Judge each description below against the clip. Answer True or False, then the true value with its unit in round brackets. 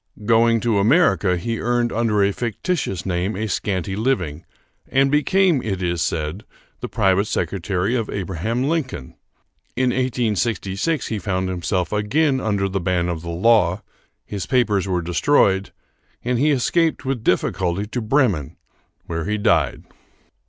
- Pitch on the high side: False (105 Hz)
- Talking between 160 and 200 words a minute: False (145 wpm)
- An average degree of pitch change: True (5.0 semitones)